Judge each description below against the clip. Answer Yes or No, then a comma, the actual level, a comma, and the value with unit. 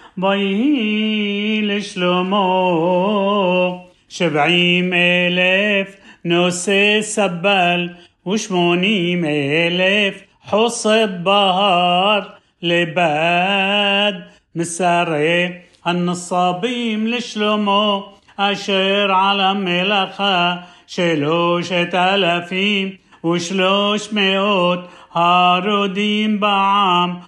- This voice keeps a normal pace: No, slow, 50 wpm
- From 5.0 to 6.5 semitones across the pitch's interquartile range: No, narrow, 2.4 semitones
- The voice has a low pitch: No, high, 190 Hz